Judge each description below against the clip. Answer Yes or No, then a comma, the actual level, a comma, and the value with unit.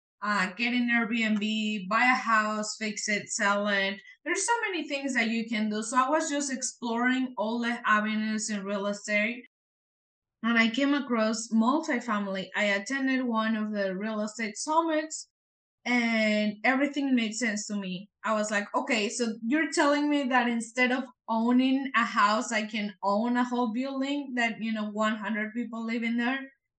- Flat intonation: No, average, 3.2 semitones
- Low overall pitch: No, high, 230 Hz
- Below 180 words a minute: Yes, average, 170 wpm